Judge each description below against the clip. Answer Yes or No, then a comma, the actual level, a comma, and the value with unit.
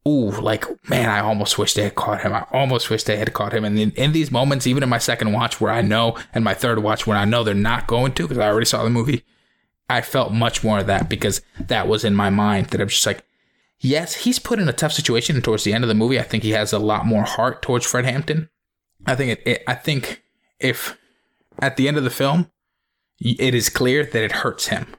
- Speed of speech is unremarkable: No, fast, 260 wpm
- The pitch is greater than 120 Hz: No, low, 115 Hz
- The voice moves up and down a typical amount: Yes, average, 3.5 semitones